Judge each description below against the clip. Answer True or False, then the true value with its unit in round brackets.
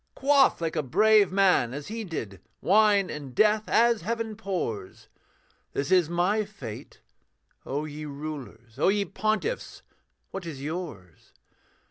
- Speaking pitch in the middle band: True (180 Hz)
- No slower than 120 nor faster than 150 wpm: True (135 wpm)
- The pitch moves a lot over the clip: True (6.9 semitones)